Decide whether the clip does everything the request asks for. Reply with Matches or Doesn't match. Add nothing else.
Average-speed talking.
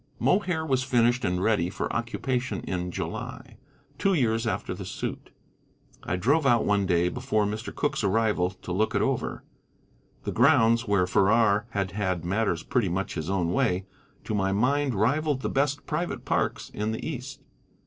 Matches